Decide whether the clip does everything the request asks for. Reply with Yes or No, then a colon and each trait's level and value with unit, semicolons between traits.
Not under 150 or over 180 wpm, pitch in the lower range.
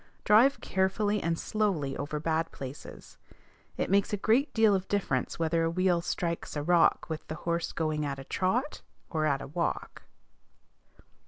No: average, 165 wpm; medium, 170 Hz